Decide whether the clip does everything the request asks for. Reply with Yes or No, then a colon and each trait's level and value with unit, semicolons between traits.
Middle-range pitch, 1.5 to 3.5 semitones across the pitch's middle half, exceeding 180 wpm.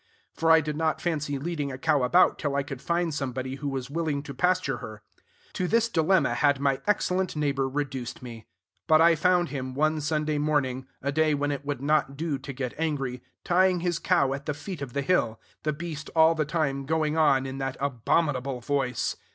Yes: medium, 145 Hz; average, 3.0 semitones; fast, 205 wpm